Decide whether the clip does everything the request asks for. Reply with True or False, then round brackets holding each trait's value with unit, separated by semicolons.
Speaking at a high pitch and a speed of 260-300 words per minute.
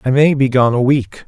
False (130 Hz; 285 wpm)